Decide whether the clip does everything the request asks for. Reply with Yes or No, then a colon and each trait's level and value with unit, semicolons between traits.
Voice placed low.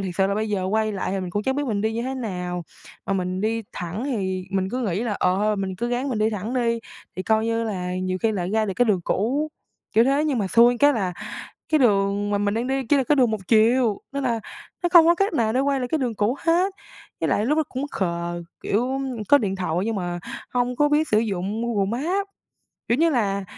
No: high, 220 Hz